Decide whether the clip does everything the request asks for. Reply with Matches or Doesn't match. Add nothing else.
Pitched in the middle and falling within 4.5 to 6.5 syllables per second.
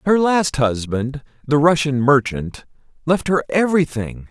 Doesn't match